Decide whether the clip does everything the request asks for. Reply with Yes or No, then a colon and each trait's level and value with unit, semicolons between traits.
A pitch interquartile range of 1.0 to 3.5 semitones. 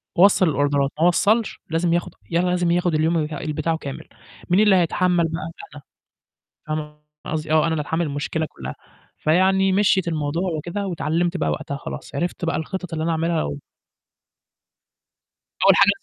Yes: average, 2.7 semitones